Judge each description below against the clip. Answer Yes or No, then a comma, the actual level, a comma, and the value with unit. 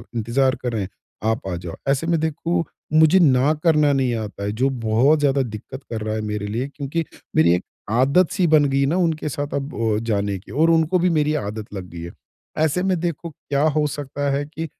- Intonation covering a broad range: Yes, wide, 6.2 semitones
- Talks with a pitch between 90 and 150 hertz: Yes, medium, 140 Hz